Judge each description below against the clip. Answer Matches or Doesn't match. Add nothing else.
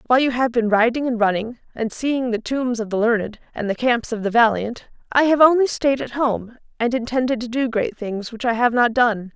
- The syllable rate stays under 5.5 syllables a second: Matches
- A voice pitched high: Matches